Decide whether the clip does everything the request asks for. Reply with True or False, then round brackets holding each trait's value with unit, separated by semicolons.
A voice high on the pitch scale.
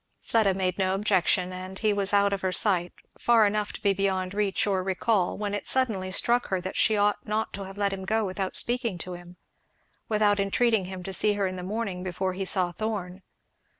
True (195 Hz)